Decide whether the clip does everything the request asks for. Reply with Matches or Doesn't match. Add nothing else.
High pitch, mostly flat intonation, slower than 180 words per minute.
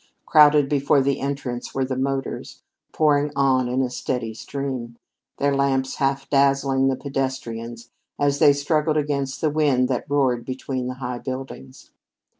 Doesn't match